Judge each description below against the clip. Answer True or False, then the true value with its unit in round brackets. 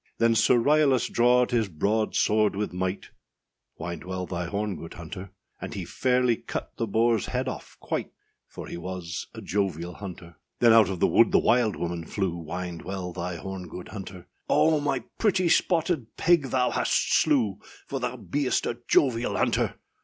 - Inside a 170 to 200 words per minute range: True (175 wpm)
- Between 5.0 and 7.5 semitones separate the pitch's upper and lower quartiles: True (5.5 semitones)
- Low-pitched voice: True (105 Hz)